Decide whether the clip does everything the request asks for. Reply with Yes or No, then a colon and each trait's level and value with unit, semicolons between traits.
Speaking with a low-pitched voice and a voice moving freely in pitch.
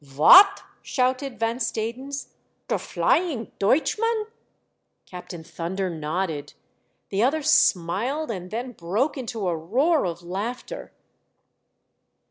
No: high, 230 Hz; wide, 7.4 semitones